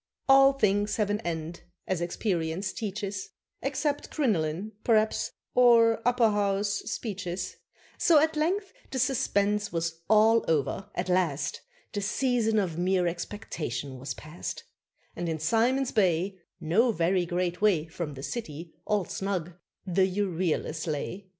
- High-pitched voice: Yes, high, 195 Hz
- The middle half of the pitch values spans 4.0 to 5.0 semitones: Yes, average, 4.6 semitones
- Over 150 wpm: No, slow, 135 wpm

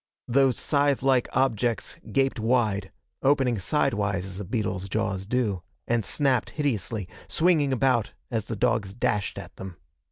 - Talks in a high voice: No, low, 115 Hz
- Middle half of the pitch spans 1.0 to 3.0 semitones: No, average, 5.0 semitones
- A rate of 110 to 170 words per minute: Yes, average, 140 wpm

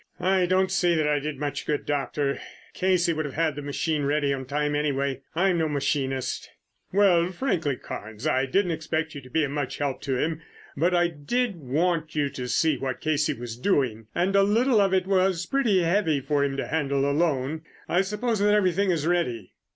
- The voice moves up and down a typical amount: Yes, average, 4.5 semitones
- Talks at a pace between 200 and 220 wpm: Yes, fast, 205 wpm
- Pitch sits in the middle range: Yes, medium, 155 Hz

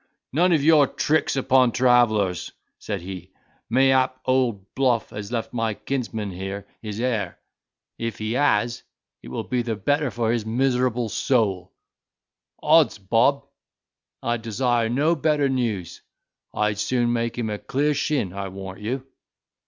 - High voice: No, low, 120 Hz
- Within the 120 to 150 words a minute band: Yes, average, 145 wpm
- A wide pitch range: No, average, 3.8 semitones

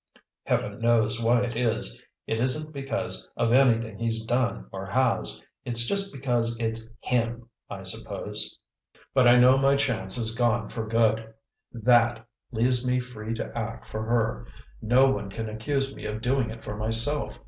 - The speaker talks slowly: No, average, 165 wpm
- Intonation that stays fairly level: Yes, narrow, 2.0 semitones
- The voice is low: Yes, low, 115 Hz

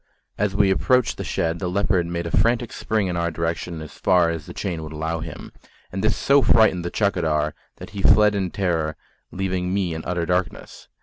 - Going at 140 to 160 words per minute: No, fast, 205 wpm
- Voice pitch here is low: Yes, very low, 90 Hz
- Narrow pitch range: No, average, 3.3 semitones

